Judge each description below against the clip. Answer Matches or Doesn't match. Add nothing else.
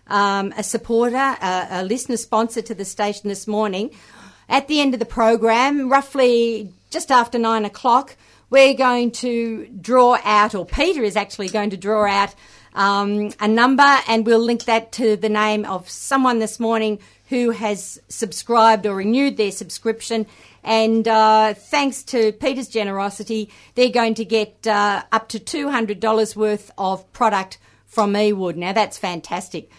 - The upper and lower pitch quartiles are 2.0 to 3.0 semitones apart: Matches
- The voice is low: Doesn't match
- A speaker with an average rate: Matches